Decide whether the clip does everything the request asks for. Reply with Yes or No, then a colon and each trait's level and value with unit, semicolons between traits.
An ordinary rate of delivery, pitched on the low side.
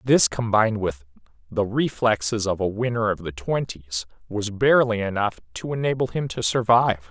Yes: average, 160 wpm; low, 110 Hz